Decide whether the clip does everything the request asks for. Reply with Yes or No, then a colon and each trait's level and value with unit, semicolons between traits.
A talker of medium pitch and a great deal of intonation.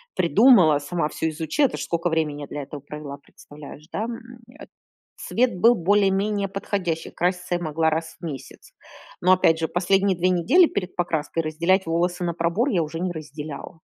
No: medium, 175 Hz; average, 3.5 semitones